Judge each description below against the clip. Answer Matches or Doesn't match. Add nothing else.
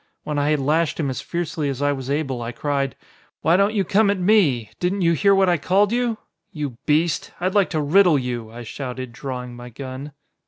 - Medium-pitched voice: Matches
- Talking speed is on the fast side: Matches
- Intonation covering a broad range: Matches